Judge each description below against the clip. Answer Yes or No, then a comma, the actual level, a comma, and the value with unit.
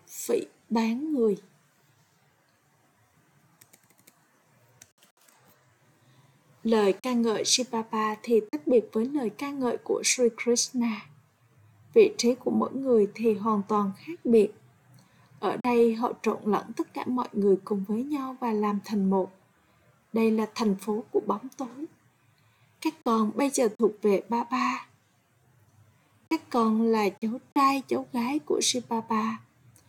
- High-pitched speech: Yes, high, 225 Hz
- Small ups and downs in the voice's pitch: No, average, 4.2 semitones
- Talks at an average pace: No, slow, 135 wpm